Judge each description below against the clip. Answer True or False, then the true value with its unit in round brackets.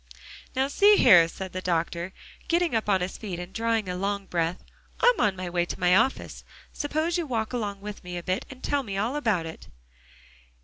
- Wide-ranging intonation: True (6.1 semitones)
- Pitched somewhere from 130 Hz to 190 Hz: False (200 Hz)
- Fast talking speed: True (210 wpm)